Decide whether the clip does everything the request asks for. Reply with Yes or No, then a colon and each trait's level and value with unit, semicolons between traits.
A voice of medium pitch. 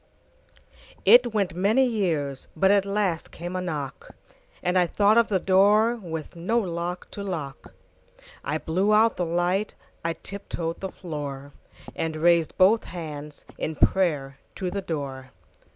Yes: medium, 180 Hz